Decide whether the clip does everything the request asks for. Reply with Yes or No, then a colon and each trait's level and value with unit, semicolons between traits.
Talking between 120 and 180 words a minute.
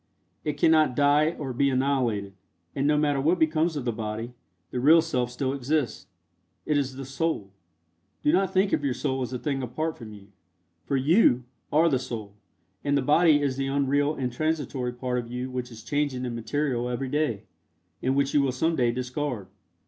No: average, 195 wpm